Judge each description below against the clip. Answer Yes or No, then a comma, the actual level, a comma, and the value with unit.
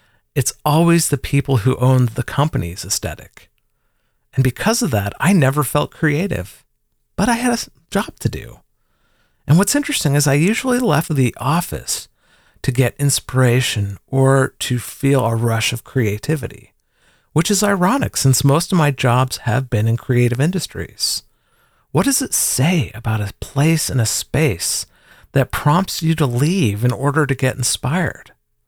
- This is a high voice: No, low, 135 Hz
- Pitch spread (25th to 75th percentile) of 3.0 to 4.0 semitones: No, average, 4.5 semitones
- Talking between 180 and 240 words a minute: No, average, 160 wpm